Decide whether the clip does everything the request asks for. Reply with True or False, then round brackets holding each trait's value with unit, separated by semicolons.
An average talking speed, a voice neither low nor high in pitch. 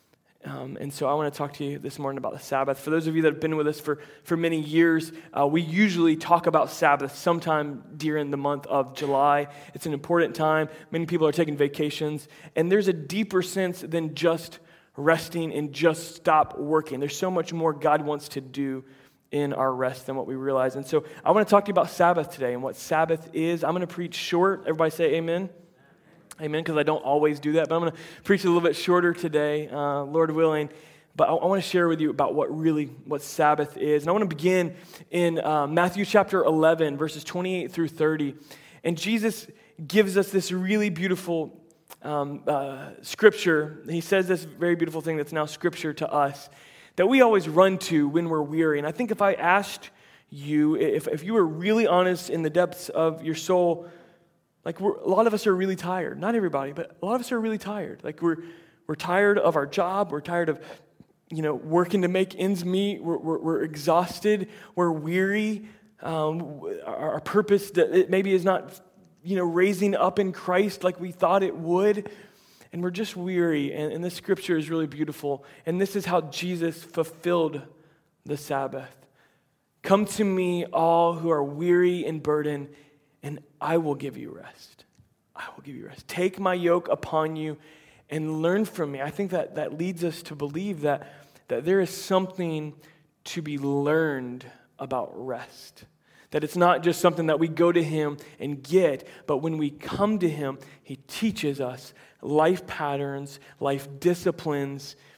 True (195 wpm; 165 Hz)